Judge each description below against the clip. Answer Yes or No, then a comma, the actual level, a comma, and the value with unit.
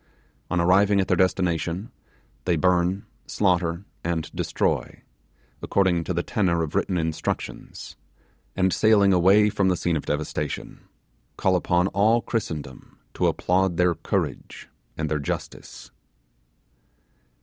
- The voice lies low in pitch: Yes, very low, 90 Hz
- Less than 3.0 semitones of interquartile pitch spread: Yes, narrow, 2.4 semitones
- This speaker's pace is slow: Yes, slow, 125 wpm